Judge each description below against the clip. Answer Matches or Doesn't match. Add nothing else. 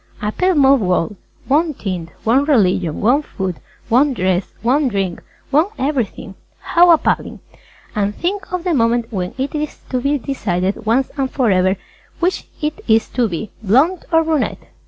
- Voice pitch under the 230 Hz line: Doesn't match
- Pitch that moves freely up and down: Matches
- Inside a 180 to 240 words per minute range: Doesn't match